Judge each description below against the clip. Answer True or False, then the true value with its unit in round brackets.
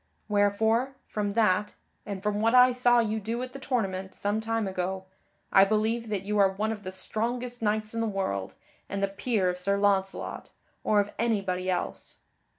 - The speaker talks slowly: False (185 wpm)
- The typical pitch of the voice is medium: False (210 Hz)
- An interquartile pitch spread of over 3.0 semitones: False (2.7 semitones)